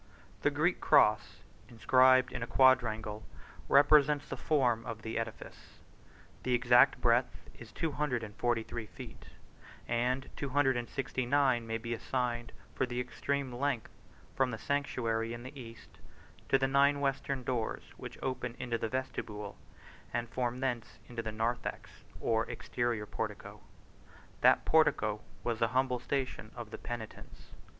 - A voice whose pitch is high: No, low, 125 Hz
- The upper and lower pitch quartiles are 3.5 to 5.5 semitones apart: No, narrow, 2.6 semitones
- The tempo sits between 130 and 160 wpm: Yes, average, 150 wpm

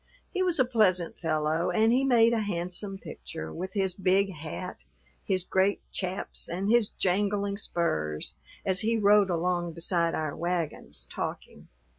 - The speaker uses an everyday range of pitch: Yes, average, 3.4 semitones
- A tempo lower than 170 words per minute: Yes, average, 150 wpm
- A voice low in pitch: No, medium, 185 Hz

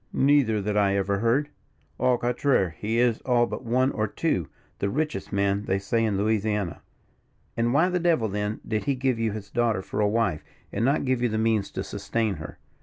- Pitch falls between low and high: No, low, 110 Hz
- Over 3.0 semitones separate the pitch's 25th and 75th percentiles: Yes, average, 3.5 semitones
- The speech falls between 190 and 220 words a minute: Yes, fast, 205 wpm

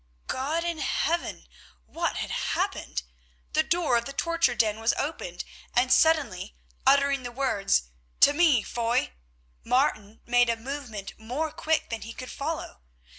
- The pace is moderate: Yes, average, 145 wpm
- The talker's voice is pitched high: Yes, very high, 255 Hz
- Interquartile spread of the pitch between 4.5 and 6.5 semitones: Yes, average, 5.1 semitones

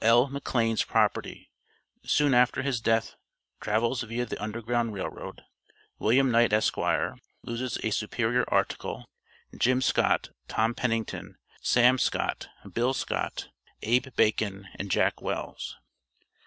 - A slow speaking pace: Yes, slow, 120 wpm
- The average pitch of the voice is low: Yes, low, 115 Hz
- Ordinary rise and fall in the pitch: No, narrow, 2.2 semitones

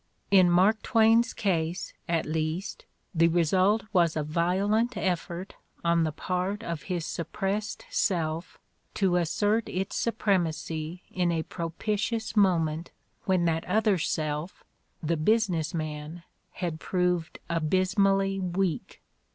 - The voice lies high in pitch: No, medium, 180 Hz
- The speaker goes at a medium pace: No, slow, 120 wpm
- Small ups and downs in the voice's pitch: No, average, 3.1 semitones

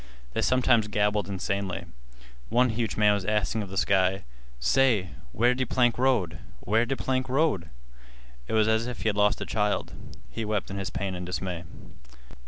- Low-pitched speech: Yes, low, 105 Hz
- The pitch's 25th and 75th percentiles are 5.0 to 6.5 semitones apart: No, average, 3.7 semitones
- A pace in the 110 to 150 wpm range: No, average, 180 wpm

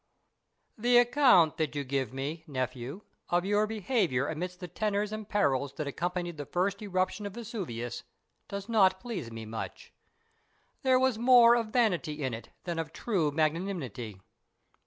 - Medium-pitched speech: Yes, medium, 180 Hz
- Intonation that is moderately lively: No, wide, 7.1 semitones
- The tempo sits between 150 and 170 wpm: Yes, average, 155 wpm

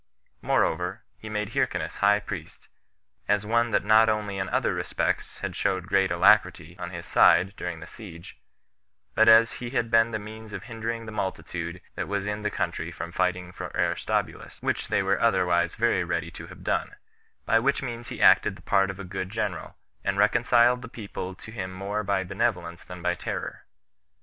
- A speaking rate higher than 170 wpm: Yes, average, 190 wpm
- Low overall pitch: Yes, low, 100 Hz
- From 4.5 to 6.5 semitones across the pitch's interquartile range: No, average, 3.5 semitones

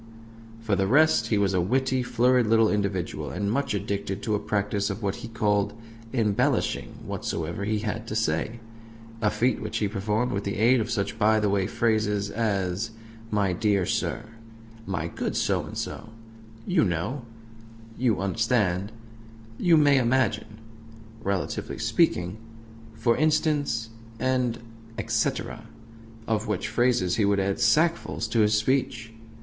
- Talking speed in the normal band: Yes, average, 150 wpm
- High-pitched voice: No, low, 110 Hz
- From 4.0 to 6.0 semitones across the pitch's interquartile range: No, average, 2.9 semitones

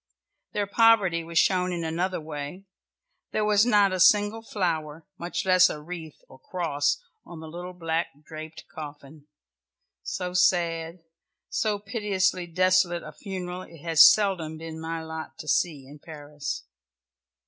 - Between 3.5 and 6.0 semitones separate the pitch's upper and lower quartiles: No, average, 2.8 semitones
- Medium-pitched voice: Yes, medium, 170 Hz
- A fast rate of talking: No, average, 145 wpm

